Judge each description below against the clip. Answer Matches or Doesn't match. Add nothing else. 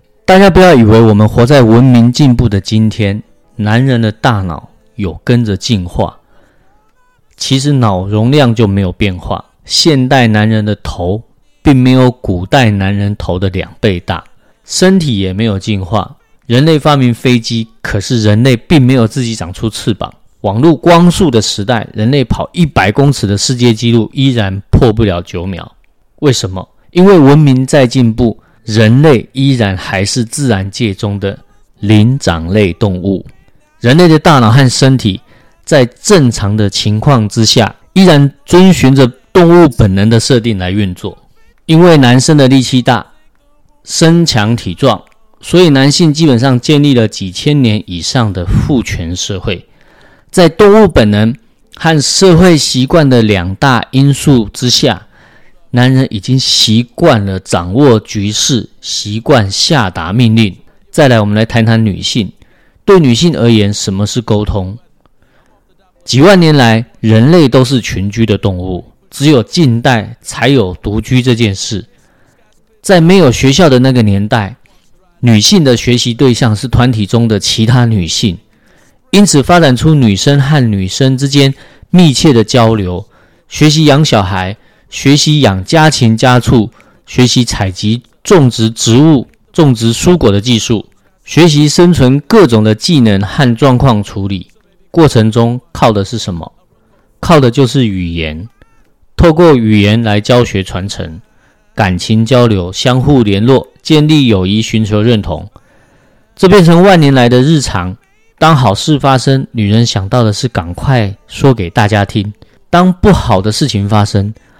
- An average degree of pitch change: Matches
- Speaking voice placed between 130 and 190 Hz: Doesn't match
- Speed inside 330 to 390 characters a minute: Doesn't match